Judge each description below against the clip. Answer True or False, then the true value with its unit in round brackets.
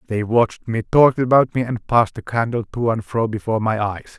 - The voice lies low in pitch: True (115 Hz)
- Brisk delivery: True (230 wpm)